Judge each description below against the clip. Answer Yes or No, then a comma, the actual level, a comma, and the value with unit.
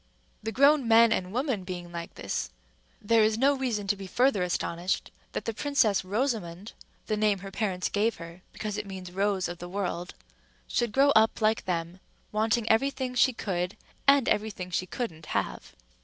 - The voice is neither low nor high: No, high, 210 Hz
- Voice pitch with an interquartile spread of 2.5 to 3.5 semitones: No, average, 4.2 semitones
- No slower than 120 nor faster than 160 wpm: No, average, 175 wpm